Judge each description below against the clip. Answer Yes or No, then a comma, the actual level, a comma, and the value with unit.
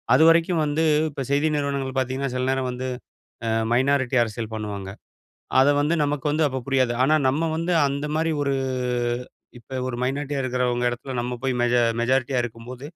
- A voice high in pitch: No, low, 135 Hz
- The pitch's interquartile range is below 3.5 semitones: Yes, narrow, 2.6 semitones